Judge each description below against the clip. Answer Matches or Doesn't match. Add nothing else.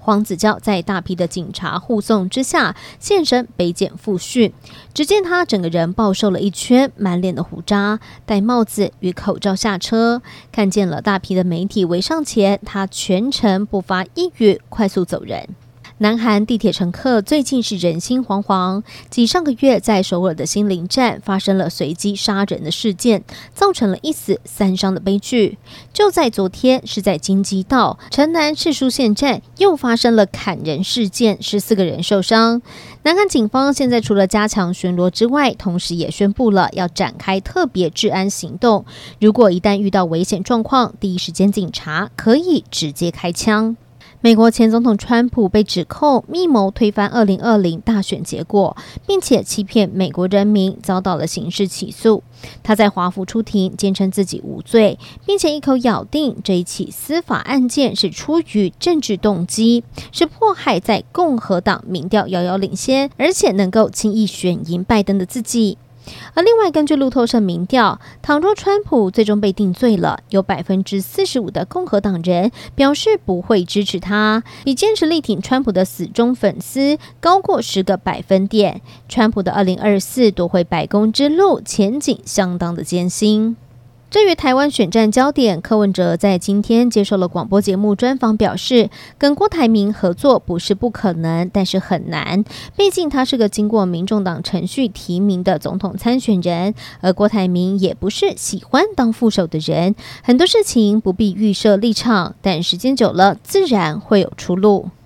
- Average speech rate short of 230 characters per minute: Doesn't match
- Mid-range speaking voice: Doesn't match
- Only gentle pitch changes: Doesn't match